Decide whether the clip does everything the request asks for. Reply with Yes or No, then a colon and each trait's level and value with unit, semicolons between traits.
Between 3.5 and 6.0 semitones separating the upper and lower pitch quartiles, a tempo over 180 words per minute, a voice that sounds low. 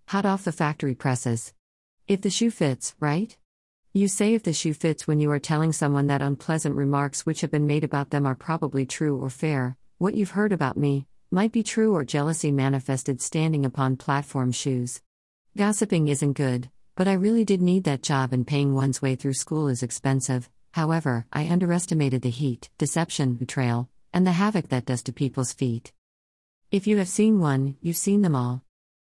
No: average, 4.5 semitones; average, 190 wpm; medium, 145 Hz